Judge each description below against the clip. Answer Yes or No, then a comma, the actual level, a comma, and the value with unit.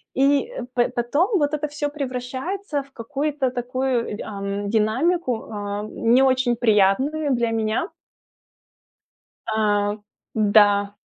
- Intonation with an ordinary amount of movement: Yes, average, 5.0 semitones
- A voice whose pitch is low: No, very high, 250 Hz